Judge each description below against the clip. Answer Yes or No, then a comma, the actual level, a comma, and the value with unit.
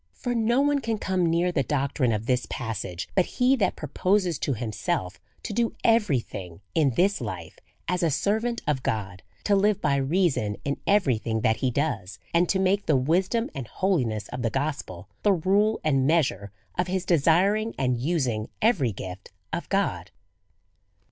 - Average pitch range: No, wide, 8.2 semitones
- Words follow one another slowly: No, average, 175 wpm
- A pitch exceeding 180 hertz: No, medium, 155 Hz